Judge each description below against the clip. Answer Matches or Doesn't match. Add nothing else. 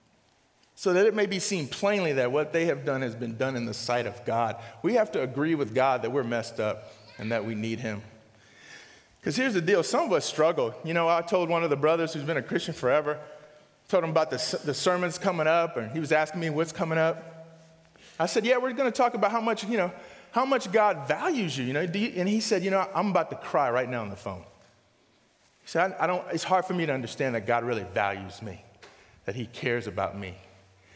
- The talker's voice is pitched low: Doesn't match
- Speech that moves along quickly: Matches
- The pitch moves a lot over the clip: Matches